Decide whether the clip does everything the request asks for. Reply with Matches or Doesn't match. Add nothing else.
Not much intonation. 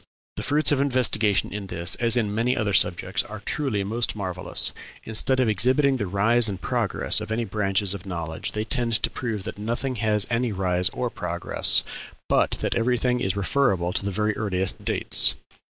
Doesn't match